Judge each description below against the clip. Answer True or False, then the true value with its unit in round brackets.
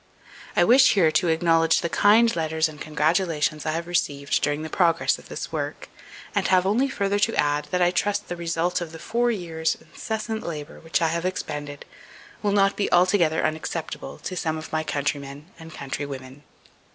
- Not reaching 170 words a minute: False (185 wpm)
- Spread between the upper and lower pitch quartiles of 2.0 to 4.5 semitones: True (3.7 semitones)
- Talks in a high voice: False (165 Hz)